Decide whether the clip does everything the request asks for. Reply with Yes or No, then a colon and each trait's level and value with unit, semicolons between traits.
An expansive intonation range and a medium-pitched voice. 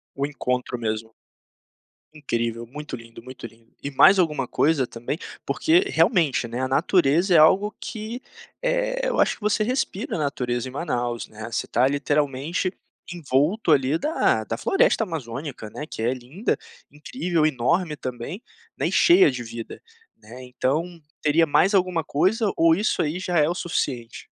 Yes: wide, 6.5 semitones; medium, 150 Hz